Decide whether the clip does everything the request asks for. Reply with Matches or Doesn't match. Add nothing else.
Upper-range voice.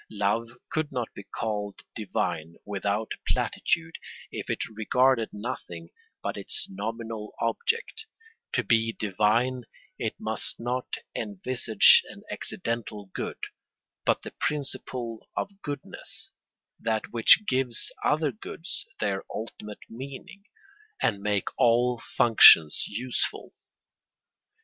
Doesn't match